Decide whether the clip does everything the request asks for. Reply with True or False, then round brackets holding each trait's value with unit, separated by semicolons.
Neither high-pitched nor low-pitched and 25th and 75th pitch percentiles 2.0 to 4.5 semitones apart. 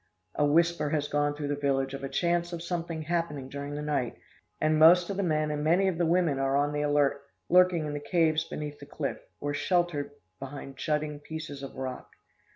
True (150 Hz; 2.7 semitones)